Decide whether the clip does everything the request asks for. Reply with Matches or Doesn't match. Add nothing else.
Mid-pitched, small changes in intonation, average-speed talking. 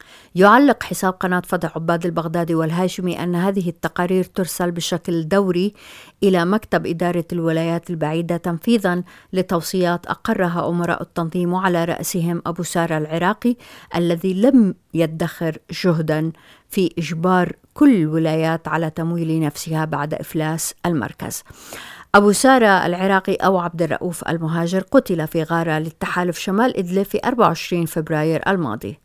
Matches